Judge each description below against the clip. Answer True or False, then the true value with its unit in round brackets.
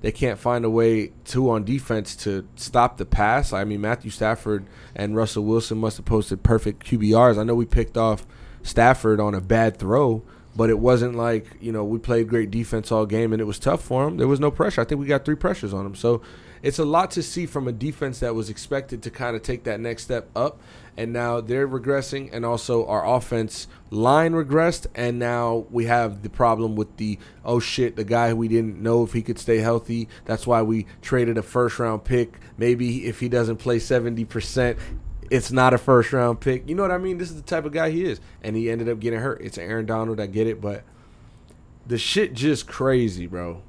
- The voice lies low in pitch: True (115 Hz)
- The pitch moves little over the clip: True (2.3 semitones)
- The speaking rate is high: True (225 wpm)